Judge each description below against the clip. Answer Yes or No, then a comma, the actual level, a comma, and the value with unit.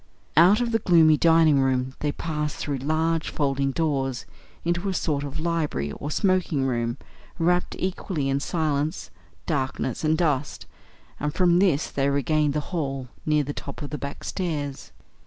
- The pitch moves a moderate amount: Yes, average, 3.2 semitones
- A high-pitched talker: No, medium, 150 Hz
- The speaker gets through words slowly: No, average, 160 wpm